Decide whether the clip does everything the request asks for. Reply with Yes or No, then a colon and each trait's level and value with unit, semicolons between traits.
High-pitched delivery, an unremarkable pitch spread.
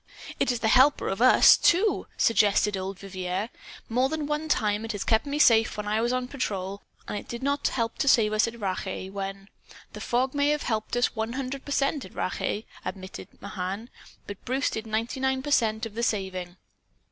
Yes: high, 225 Hz; average, 4.7 semitones